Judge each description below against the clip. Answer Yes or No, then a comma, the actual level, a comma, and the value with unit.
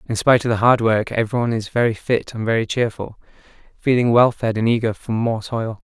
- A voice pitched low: Yes, low, 115 Hz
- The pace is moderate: No, fast, 215 wpm